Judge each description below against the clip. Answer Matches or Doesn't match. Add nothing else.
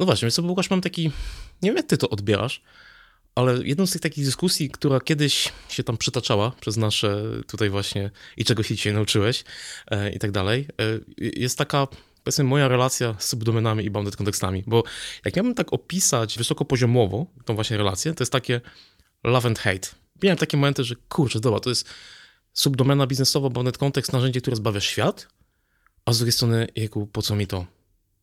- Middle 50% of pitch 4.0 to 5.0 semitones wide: Matches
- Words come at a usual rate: Doesn't match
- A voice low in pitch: Matches